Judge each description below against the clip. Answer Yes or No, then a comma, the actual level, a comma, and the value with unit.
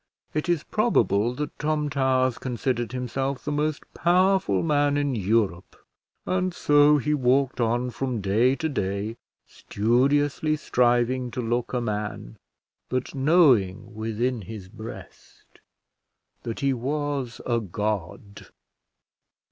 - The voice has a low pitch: Yes, low, 125 Hz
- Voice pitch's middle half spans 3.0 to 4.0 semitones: No, average, 4.4 semitones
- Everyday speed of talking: No, slow, 120 wpm